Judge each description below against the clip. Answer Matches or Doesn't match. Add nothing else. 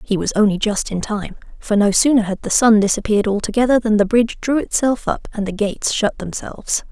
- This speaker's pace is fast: Matches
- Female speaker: Matches